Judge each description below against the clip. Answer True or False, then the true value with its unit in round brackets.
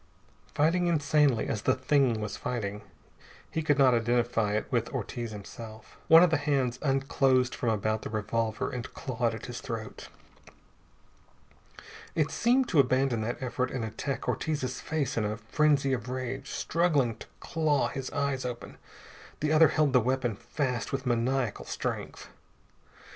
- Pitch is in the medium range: False (130 Hz)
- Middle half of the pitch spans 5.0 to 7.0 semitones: False (3.8 semitones)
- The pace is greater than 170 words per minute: False (155 wpm)